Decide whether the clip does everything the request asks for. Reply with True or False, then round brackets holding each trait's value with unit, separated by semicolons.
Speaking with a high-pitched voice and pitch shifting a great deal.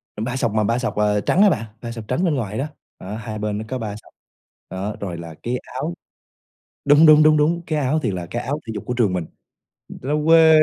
False (120 Hz; 6.1 semitones)